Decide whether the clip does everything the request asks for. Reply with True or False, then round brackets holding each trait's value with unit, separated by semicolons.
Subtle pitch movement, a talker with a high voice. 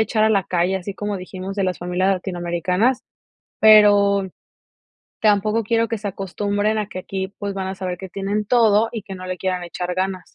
True (2.3 semitones; 195 Hz)